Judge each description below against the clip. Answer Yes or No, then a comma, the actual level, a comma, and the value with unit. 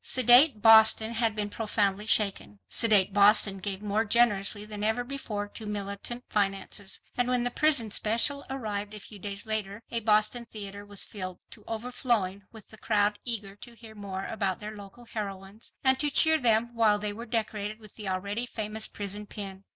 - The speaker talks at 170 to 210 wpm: Yes, average, 180 wpm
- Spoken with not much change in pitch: Yes, narrow, 2.3 semitones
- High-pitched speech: Yes, high, 215 Hz